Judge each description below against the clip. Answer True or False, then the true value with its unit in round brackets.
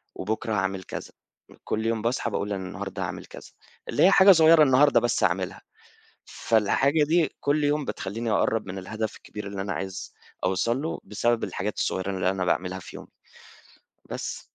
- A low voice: True (105 Hz)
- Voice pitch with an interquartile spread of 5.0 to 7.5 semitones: True (5.6 semitones)